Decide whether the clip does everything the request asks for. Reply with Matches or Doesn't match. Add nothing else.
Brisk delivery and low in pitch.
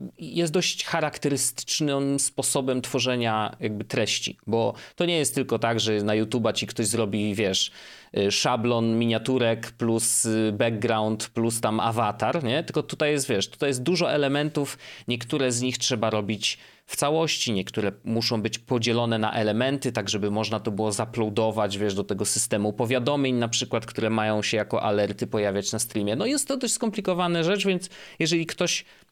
Matches